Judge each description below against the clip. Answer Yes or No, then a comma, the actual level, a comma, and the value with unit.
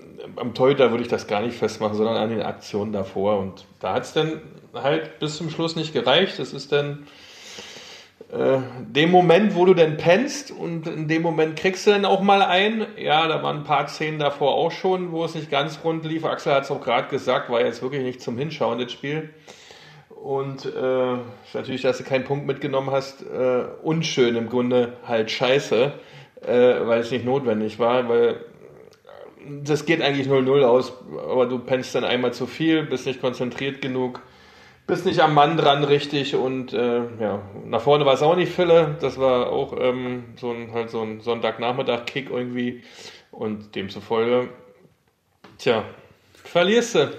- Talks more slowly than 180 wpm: No, average, 185 wpm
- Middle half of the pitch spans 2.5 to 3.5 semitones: No, average, 4.2 semitones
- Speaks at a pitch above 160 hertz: No, low, 135 Hz